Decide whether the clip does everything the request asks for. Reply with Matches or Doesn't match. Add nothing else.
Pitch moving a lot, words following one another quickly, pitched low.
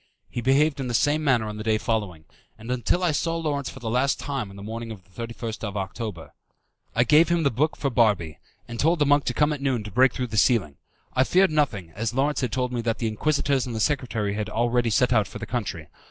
Doesn't match